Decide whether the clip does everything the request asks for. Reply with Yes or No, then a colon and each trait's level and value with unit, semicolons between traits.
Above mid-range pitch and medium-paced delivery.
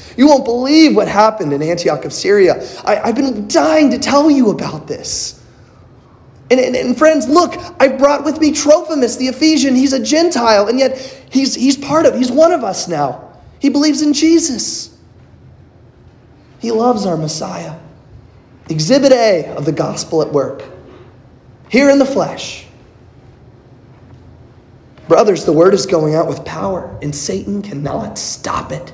Yes: high, 235 Hz; average, 160 wpm